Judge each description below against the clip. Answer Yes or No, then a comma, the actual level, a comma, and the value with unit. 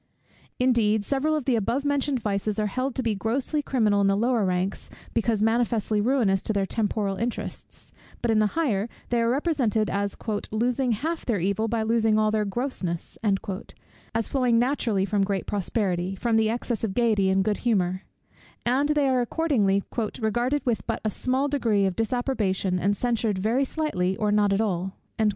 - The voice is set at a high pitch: Yes, high, 220 Hz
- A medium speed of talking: Yes, average, 180 wpm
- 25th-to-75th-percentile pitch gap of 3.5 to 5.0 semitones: Yes, average, 3.8 semitones